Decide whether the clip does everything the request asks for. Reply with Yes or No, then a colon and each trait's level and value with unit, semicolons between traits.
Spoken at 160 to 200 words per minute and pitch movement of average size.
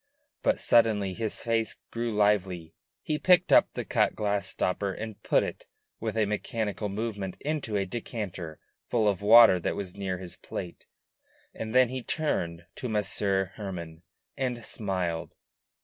No: average, 150 wpm; average, 3.5 semitones